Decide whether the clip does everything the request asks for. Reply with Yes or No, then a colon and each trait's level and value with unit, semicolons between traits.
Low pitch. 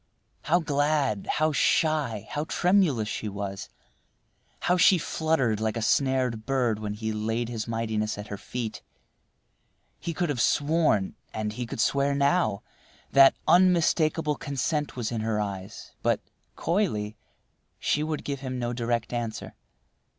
Yes: low, 125 Hz